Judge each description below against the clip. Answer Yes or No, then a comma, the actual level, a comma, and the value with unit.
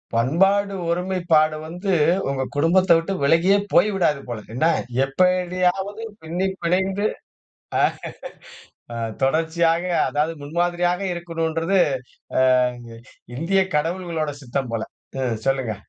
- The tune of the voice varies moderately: Yes, average, 3.4 semitones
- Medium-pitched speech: Yes, medium, 170 Hz